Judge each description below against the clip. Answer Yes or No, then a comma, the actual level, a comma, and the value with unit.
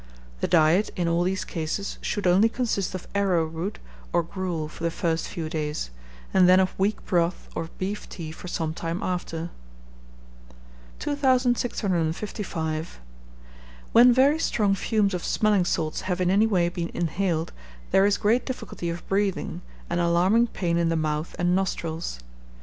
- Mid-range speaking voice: Yes, medium, 180 Hz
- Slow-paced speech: No, average, 155 wpm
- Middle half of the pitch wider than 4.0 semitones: No, average, 3.3 semitones